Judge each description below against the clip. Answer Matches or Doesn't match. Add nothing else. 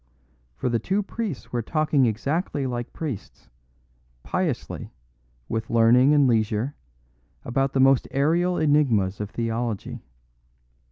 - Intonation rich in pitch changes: Doesn't match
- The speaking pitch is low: Matches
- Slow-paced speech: Matches